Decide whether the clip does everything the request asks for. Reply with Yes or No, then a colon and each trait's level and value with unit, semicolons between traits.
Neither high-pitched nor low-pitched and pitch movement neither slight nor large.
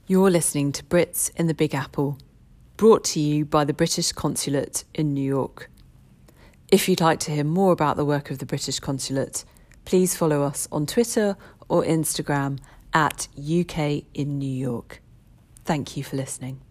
Yes: medium, 145 Hz; average, 3.4 semitones